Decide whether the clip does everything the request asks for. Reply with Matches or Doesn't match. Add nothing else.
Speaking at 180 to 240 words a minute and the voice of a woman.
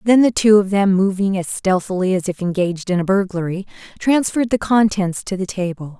Matches